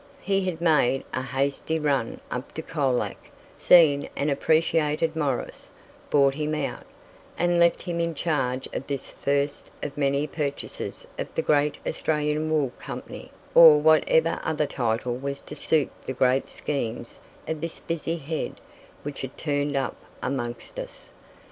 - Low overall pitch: No, medium, 150 Hz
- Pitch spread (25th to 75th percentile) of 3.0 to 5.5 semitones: No, narrow, 2.6 semitones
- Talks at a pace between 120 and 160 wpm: Yes, average, 150 wpm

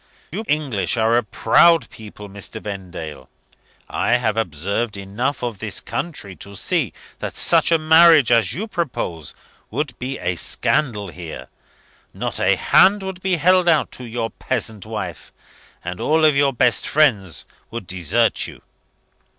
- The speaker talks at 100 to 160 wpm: Yes, average, 150 wpm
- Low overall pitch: Yes, low, 115 Hz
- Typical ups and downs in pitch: No, wide, 7.6 semitones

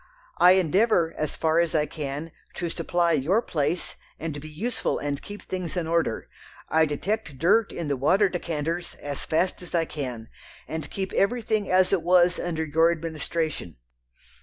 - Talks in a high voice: No, medium, 165 Hz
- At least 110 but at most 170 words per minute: Yes, average, 165 wpm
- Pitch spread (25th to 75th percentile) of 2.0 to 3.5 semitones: Yes, average, 3.2 semitones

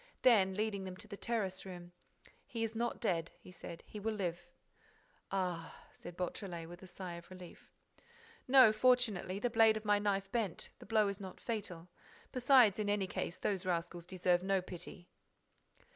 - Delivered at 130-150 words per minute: No, average, 175 wpm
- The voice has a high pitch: Yes, high, 195 Hz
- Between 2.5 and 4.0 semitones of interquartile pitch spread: Yes, average, 3.3 semitones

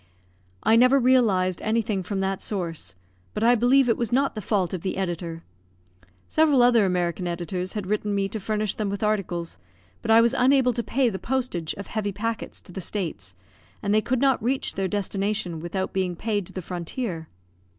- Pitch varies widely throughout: No, average, 4.2 semitones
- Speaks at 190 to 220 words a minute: Yes, average, 195 wpm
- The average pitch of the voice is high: Yes, high, 205 Hz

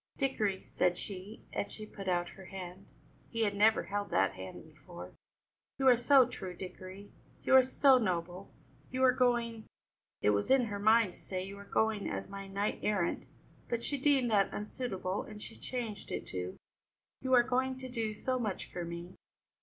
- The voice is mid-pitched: No, high, 205 Hz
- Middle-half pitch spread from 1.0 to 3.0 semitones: No, average, 4.8 semitones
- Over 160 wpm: Yes, average, 190 wpm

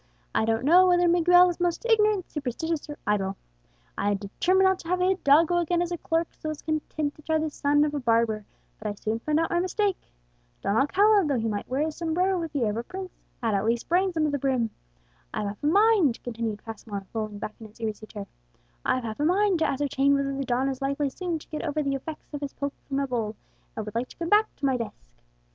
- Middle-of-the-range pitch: No, very high, 290 Hz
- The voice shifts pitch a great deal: Yes, wide, 7.0 semitones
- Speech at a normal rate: No, fast, 250 wpm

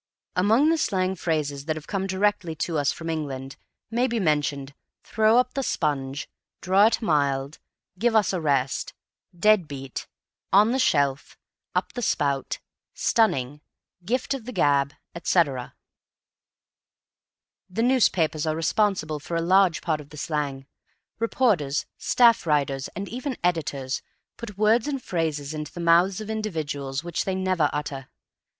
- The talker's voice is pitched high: No, medium, 165 Hz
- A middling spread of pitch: No, wide, 6.6 semitones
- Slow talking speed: No, average, 145 wpm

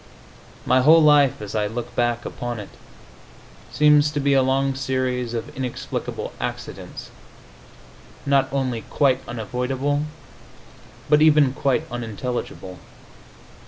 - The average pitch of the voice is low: Yes, low, 130 Hz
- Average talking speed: No, slow, 115 wpm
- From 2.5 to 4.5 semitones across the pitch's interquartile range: Yes, average, 2.8 semitones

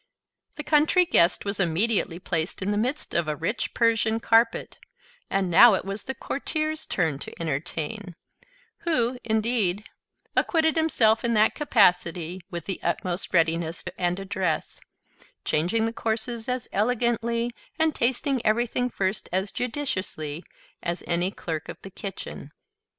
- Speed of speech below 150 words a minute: Yes, average, 140 wpm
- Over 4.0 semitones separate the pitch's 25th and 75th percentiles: Yes, average, 5.3 semitones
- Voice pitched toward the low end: No, high, 215 Hz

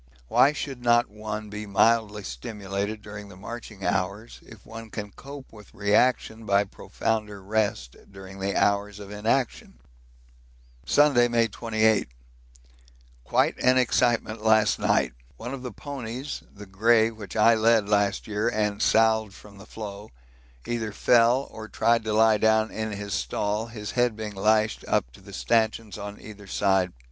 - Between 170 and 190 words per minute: No, average, 155 wpm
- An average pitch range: No, narrow, 2.0 semitones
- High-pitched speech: No, low, 110 Hz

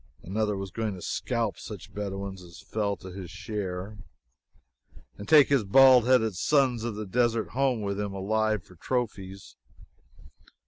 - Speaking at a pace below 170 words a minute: Yes, average, 150 wpm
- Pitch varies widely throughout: No, average, 3.2 semitones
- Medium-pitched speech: No, low, 105 Hz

